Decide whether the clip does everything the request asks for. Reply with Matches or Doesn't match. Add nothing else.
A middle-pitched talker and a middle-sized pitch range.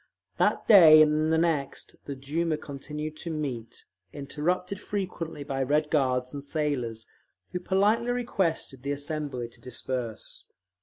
Matches